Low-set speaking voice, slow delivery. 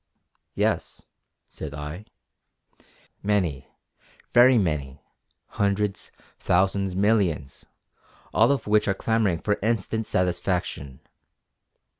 Yes: very low, 95 Hz; slow, 85 wpm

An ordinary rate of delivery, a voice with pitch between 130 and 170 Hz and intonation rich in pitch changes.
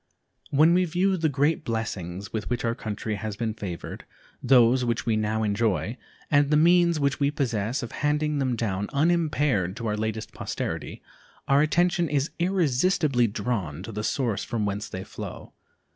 No: average, 170 wpm; low, 120 Hz; wide, 5.8 semitones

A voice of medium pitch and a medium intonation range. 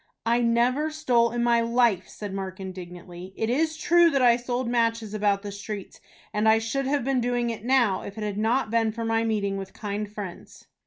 No: high, 225 Hz; average, 3.1 semitones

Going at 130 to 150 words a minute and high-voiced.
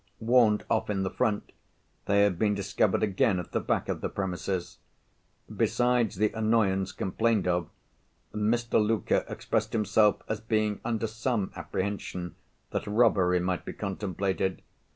No: average, 140 wpm; low, 105 Hz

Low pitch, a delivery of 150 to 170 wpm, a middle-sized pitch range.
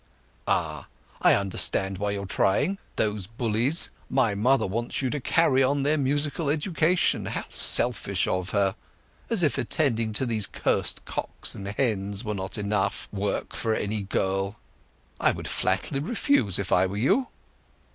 No: low, 110 Hz; average, 155 wpm; wide, 5.8 semitones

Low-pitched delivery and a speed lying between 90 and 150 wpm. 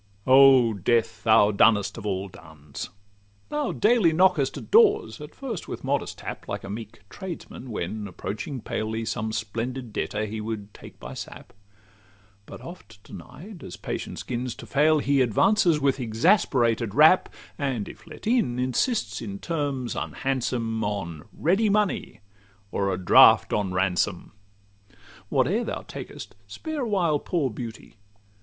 Yes: low, 120 Hz; average, 145 wpm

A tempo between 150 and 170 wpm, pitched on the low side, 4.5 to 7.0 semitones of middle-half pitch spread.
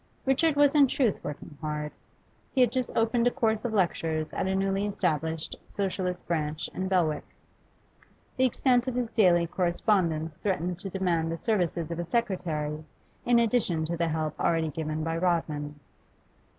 No: average, 165 wpm; medium, 180 Hz; wide, 5.6 semitones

